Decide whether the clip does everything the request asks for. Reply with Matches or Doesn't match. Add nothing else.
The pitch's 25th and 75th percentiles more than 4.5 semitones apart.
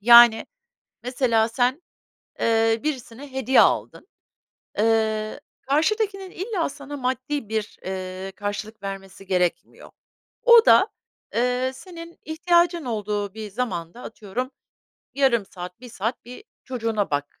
Matches